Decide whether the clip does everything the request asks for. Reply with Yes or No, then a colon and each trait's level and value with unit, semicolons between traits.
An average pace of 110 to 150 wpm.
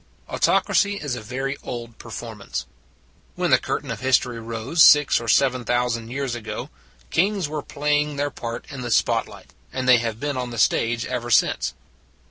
No: average, 180 wpm